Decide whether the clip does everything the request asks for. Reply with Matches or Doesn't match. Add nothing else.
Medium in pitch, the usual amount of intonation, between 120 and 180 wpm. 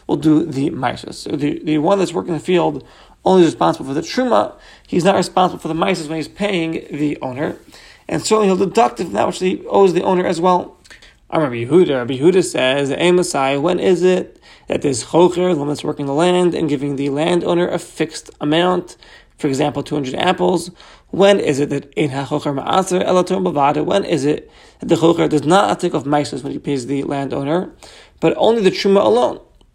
Doesn't match